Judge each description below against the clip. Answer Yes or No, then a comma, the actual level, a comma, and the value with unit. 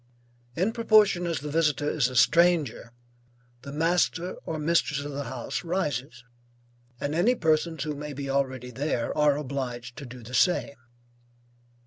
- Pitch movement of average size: Yes, average, 4.0 semitones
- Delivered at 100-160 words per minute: Yes, average, 150 wpm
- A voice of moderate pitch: Yes, medium, 150 Hz